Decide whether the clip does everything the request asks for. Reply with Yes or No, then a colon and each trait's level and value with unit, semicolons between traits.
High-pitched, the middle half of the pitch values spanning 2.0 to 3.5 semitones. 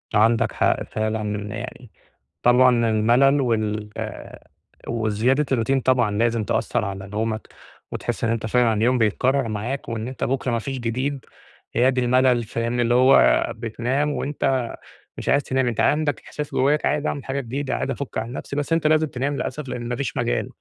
No: low, 125 Hz; average, 3.2 semitones